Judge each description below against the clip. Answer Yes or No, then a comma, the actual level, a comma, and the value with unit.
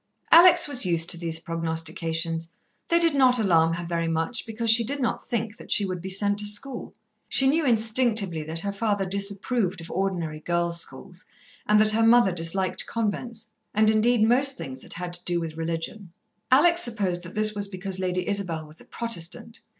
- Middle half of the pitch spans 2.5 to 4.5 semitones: No, average, 5.3 semitones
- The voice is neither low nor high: No, high, 200 Hz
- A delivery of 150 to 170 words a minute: No, average, 190 wpm